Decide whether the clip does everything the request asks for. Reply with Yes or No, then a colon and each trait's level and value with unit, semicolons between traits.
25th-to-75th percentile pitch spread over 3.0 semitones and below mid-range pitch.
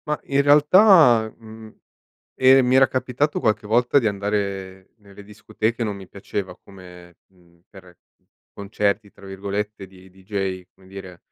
Yes: average, 3.7 semitones; low, 100 Hz